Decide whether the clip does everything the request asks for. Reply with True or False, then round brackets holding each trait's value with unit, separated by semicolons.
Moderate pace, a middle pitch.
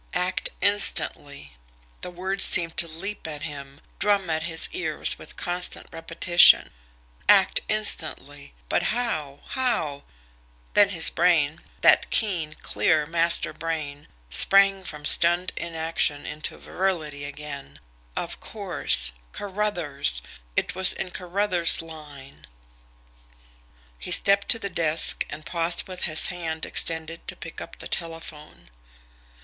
False (120 wpm; 165 Hz)